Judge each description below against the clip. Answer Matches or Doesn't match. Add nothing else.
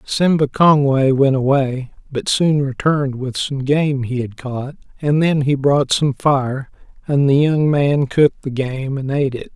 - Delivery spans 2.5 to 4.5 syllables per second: Matches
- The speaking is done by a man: Matches